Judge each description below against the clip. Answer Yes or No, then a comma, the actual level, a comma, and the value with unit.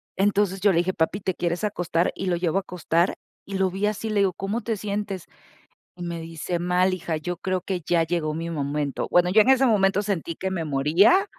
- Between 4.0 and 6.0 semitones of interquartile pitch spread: No, average, 2.9 semitones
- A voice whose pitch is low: No, medium, 185 Hz